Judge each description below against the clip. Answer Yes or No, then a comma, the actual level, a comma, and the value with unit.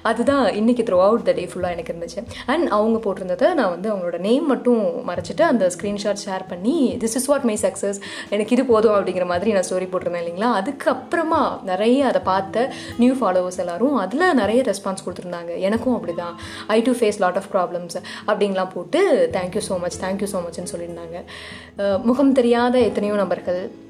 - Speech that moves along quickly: Yes, fast, 170 wpm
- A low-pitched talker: No, high, 210 Hz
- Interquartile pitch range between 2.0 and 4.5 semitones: No, average, 5.2 semitones